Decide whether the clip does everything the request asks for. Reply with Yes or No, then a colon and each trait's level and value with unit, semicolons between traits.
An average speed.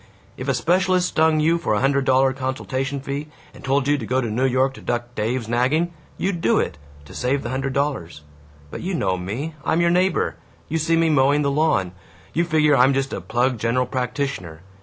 No: fast, 210 wpm